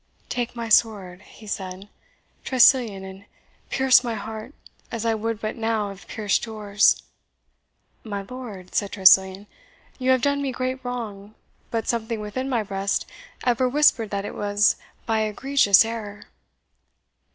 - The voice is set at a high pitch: Yes, high, 220 Hz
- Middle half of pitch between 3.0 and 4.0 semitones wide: Yes, average, 3.3 semitones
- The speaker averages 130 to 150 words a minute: Yes, average, 140 wpm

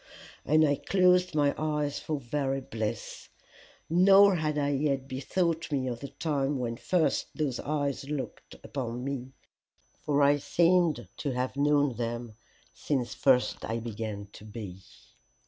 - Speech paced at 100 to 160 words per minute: Yes, average, 145 wpm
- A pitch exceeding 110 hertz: Yes, medium, 140 Hz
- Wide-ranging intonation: No, average, 3.6 semitones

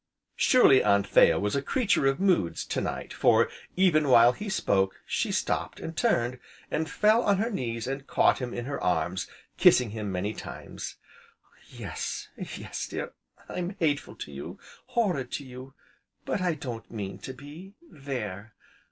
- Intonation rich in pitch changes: Yes, wide, 8.0 semitones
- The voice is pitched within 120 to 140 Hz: Yes, low, 135 Hz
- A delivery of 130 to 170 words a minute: Yes, average, 160 wpm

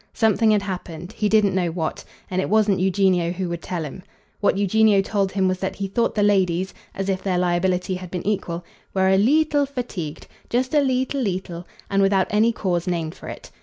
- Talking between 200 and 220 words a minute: Yes, fast, 205 wpm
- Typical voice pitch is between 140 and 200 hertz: Yes, high, 190 Hz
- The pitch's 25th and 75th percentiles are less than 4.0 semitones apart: Yes, average, 2.8 semitones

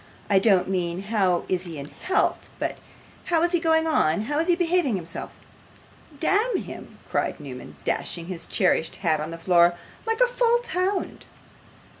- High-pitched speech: Yes, high, 205 Hz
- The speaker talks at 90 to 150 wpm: No, average, 170 wpm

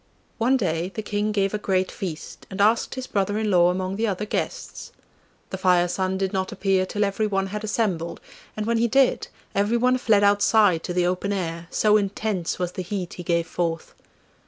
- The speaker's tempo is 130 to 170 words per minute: No, average, 195 wpm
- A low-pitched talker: No, high, 195 Hz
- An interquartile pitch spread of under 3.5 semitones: Yes, average, 2.8 semitones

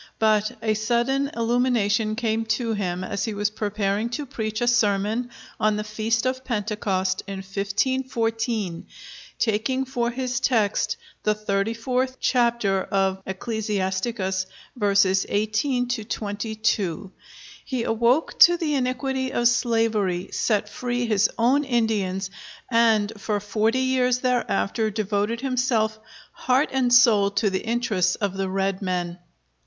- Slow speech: Yes, slow, 130 wpm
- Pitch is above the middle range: Yes, high, 220 Hz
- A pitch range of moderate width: Yes, average, 3.3 semitones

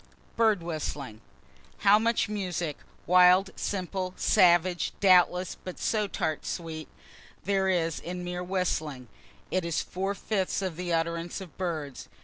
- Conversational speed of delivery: No, slow, 130 wpm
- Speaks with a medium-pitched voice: Yes, medium, 180 Hz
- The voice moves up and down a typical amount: No, narrow, 2.3 semitones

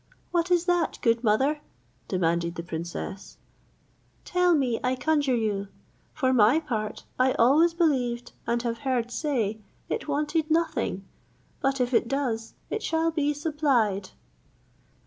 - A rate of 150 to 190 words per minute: No, slow, 135 wpm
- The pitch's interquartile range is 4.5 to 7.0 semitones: Yes, wide, 5.5 semitones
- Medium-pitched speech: No, very high, 260 Hz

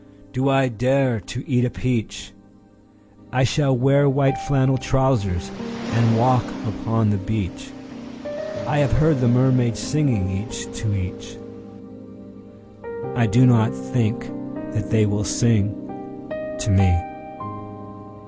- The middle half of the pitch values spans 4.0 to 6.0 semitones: Yes, average, 4.5 semitones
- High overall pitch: No, low, 120 Hz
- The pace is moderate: No, slow, 110 wpm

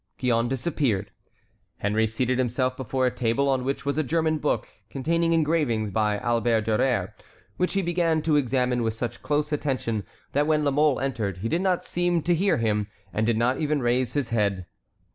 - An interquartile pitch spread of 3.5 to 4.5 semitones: No, average, 4.9 semitones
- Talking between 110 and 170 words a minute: No, average, 185 wpm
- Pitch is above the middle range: No, low, 130 Hz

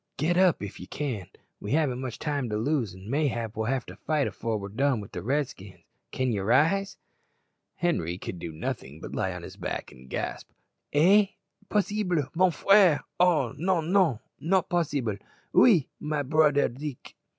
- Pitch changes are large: Yes, wide, 7.3 semitones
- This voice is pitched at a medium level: Yes, medium, 145 Hz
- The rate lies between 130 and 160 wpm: No, average, 175 wpm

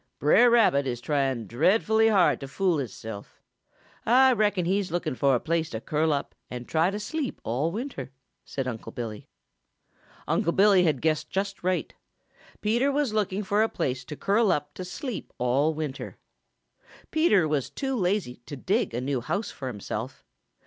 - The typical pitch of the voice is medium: Yes, medium, 160 Hz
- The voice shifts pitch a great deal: Yes, wide, 7.6 semitones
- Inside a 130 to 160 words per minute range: No, average, 170 wpm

